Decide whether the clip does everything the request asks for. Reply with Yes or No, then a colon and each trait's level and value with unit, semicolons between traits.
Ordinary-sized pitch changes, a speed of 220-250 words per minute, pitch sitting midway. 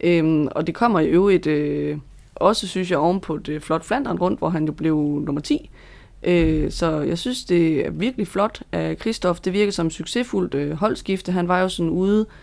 No: average, 4.0 semitones; average, 205 wpm; medium, 170 Hz